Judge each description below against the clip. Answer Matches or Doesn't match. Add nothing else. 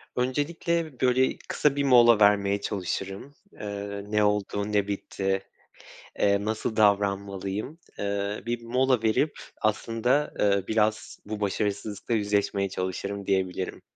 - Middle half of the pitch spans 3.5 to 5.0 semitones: Doesn't match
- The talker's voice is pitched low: Matches